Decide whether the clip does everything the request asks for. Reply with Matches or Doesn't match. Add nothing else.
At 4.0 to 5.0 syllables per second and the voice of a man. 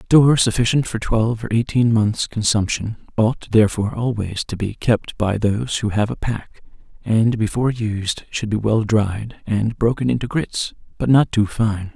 Matches